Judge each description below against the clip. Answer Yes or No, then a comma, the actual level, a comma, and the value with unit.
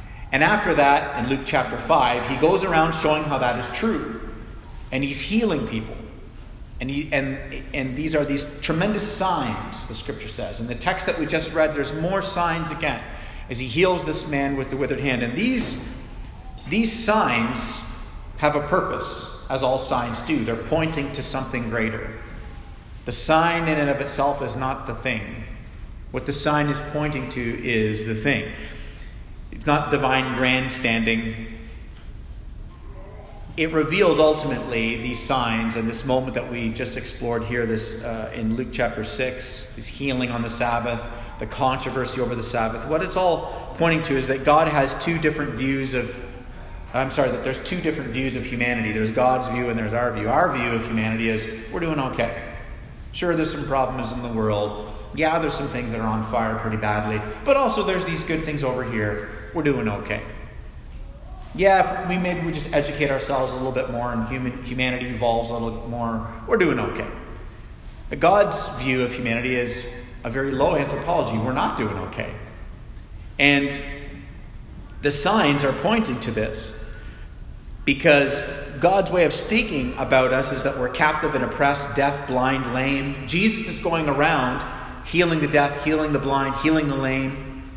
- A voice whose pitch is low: Yes, low, 130 Hz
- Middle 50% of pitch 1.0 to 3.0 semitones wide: No, average, 4.3 semitones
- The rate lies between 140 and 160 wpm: No, average, 175 wpm